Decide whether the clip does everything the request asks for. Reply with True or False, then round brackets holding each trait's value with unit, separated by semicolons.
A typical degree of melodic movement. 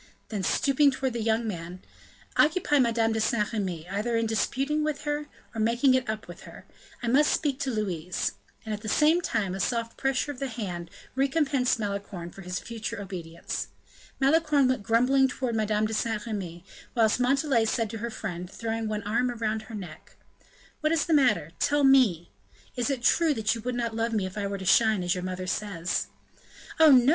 True (4.7 semitones)